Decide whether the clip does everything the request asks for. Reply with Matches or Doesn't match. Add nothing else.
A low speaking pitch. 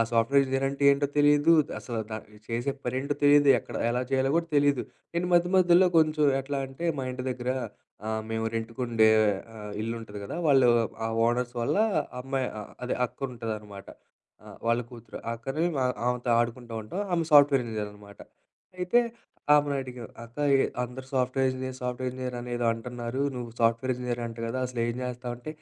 Matches